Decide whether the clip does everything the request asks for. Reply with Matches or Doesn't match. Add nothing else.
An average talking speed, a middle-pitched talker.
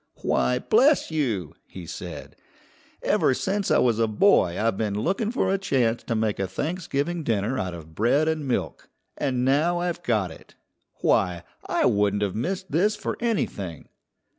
Doesn't match